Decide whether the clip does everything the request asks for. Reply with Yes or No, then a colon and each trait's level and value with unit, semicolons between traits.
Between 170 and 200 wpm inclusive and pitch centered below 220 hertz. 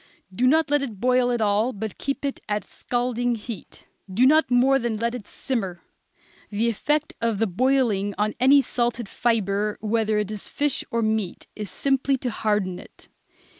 No: average, 180 wpm; high, 230 Hz